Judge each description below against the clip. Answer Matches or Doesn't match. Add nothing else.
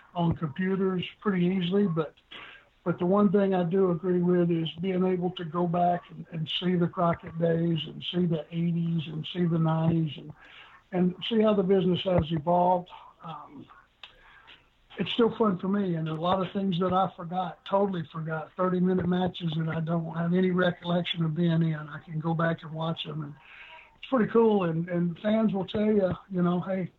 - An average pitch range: Doesn't match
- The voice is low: Doesn't match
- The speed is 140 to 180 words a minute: Doesn't match